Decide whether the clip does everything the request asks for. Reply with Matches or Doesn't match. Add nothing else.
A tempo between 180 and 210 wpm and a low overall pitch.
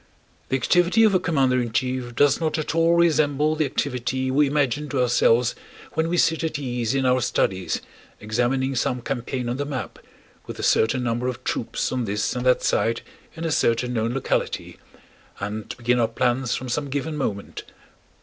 Matches